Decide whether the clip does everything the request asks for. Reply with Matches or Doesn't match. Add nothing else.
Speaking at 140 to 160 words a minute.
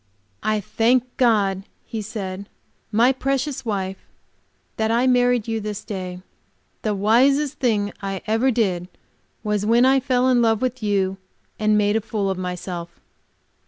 Matches